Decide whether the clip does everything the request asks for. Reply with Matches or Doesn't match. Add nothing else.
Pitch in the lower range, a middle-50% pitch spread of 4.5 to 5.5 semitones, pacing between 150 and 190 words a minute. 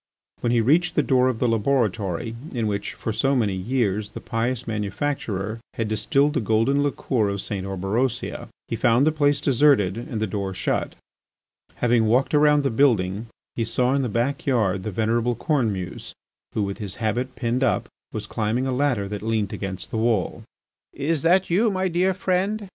Matches